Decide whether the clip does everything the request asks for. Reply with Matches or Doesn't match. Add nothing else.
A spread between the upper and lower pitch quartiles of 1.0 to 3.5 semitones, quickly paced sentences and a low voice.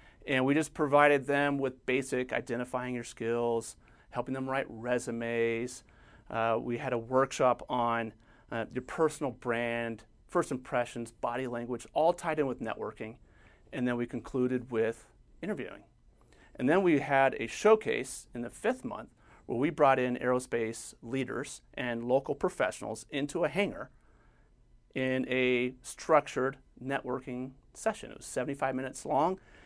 Doesn't match